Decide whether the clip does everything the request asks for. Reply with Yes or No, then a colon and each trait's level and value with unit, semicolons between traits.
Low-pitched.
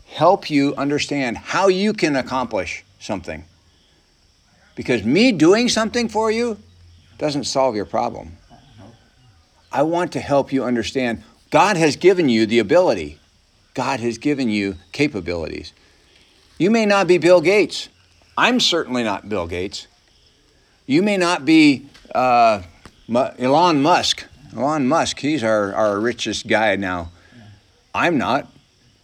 Yes: low, 120 Hz